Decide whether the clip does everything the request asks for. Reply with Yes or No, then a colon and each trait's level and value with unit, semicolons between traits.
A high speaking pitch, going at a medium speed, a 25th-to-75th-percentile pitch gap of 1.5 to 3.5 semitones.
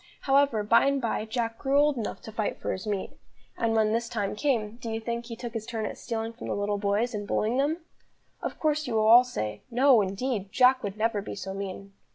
No: high, 225 Hz; fast, 235 wpm; average, 3.2 semitones